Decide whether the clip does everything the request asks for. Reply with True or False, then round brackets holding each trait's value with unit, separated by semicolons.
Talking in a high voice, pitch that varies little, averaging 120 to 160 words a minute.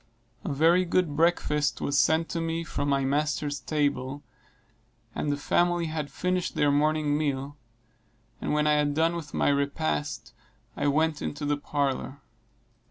False (150 Hz; 2.1 semitones; 155 wpm)